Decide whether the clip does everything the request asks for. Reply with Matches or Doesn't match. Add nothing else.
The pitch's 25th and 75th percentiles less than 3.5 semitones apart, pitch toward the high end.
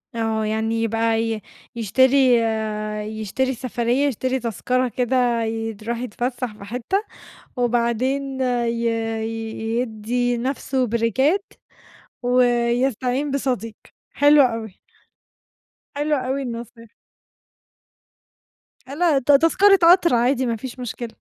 Matches